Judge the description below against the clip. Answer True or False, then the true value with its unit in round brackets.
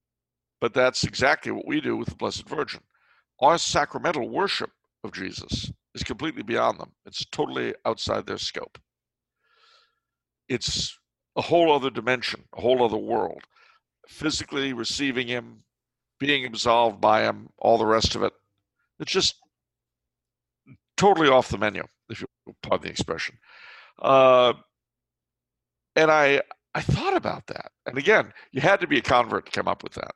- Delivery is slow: False (155 wpm)